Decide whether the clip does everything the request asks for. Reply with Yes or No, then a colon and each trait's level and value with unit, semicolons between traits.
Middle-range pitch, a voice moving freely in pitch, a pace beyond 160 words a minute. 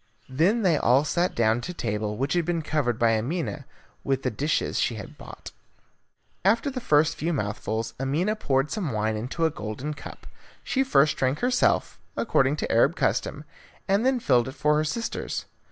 Yes: medium, 145 Hz; wide, 6.4 semitones; average, 185 wpm